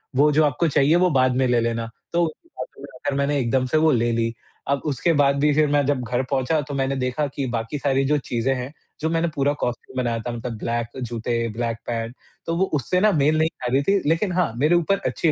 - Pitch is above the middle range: No, medium, 140 Hz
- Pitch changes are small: No, average, 4.2 semitones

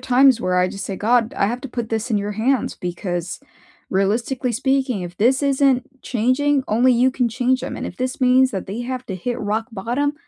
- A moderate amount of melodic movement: Yes, average, 3.9 semitones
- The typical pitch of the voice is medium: No, high, 245 Hz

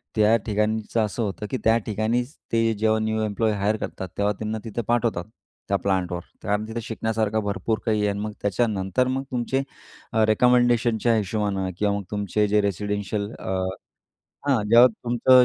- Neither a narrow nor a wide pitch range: No, narrow, 2.1 semitones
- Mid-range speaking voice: No, low, 110 Hz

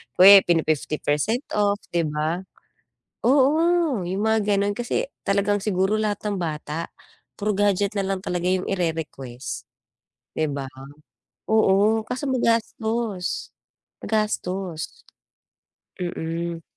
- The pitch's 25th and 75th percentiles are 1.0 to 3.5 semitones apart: No, average, 4.3 semitones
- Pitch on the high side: Yes, high, 195 Hz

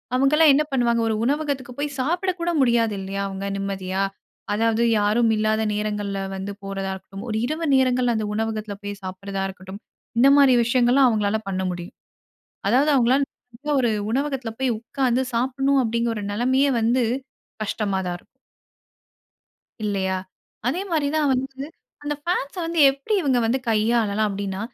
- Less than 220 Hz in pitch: No, high, 235 Hz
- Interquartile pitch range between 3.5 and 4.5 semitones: No, average, 4.9 semitones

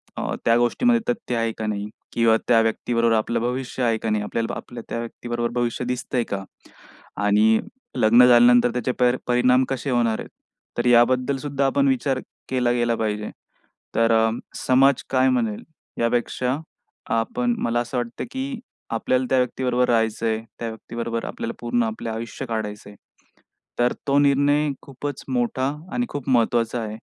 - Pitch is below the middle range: Yes, low, 120 Hz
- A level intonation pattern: Yes, narrow, 2.1 semitones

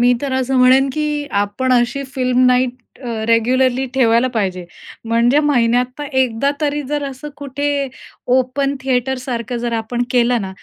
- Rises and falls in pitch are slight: Yes, narrow, 2.2 semitones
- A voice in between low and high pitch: No, very high, 255 Hz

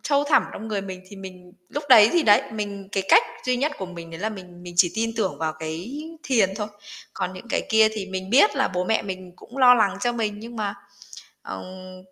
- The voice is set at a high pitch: Yes, high, 200 Hz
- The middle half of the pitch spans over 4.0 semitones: No, average, 3.7 semitones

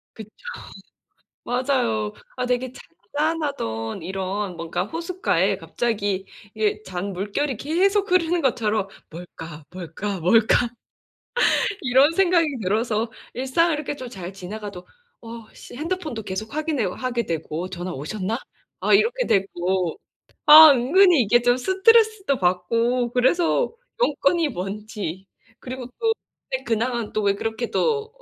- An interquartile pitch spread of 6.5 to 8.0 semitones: Yes, wide, 7.5 semitones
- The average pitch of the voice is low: No, high, 235 Hz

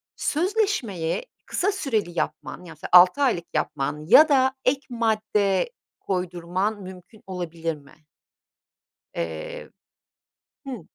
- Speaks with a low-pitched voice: No, high, 190 Hz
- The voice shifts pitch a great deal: Yes, wide, 7.2 semitones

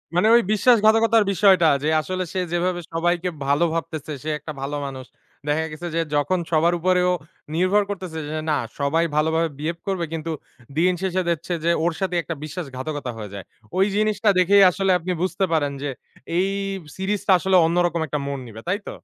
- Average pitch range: Yes, average, 3.4 semitones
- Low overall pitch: No, medium, 170 Hz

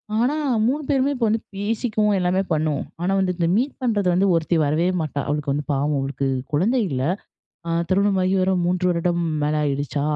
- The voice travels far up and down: Yes, wide, 5.8 semitones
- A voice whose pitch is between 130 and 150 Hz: No, medium, 180 Hz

